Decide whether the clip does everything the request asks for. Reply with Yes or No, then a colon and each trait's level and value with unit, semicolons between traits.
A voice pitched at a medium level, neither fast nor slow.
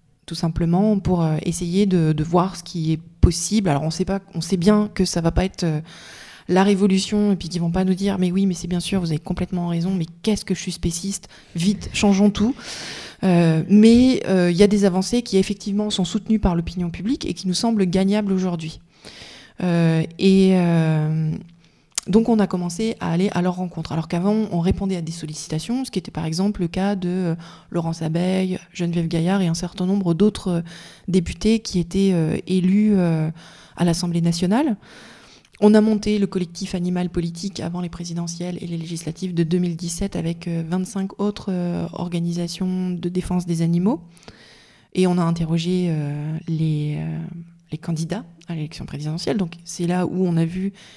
Yes: medium, 180 Hz; average, 190 wpm